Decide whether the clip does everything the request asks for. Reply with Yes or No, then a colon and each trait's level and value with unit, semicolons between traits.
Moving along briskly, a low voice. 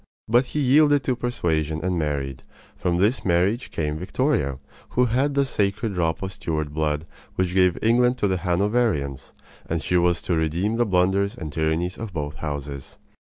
No: average, 170 wpm; very low, 90 Hz